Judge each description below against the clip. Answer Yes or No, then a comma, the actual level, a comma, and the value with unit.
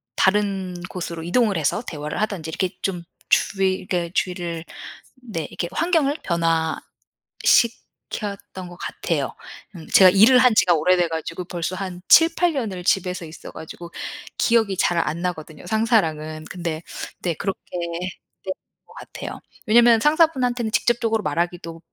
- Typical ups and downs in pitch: Yes, average, 4.5 semitones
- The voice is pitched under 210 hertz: Yes, medium, 185 Hz